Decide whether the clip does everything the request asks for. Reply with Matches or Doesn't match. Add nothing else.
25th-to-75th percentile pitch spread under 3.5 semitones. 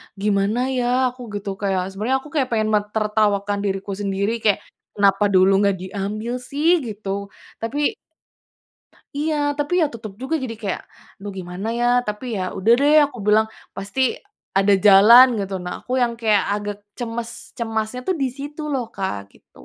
Doesn't match